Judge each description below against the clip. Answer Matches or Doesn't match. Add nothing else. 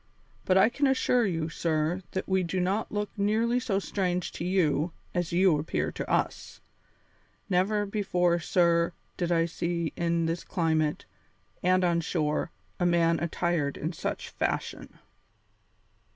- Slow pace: Doesn't match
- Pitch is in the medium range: Matches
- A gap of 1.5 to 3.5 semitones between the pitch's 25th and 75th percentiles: Matches